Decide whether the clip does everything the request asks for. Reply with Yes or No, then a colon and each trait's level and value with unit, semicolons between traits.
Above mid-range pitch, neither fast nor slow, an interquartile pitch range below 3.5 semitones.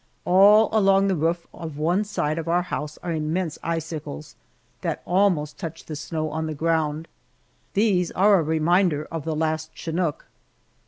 No: medium, 165 Hz; average, 160 wpm; average, 2.8 semitones